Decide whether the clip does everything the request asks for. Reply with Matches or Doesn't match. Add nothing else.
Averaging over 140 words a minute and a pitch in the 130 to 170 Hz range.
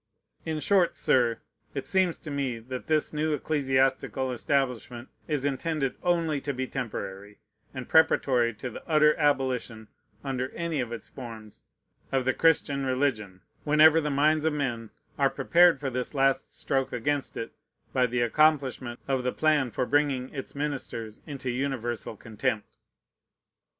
Matches